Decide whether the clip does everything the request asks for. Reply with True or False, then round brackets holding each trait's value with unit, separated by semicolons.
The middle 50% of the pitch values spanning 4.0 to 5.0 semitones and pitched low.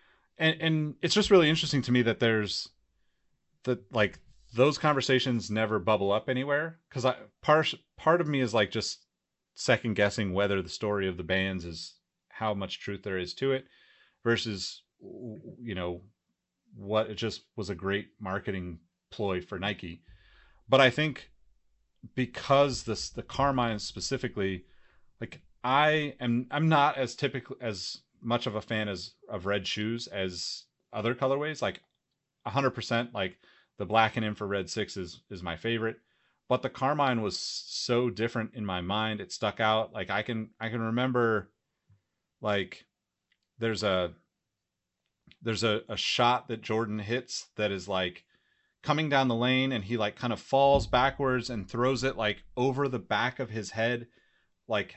True (4.3 semitones; 115 Hz)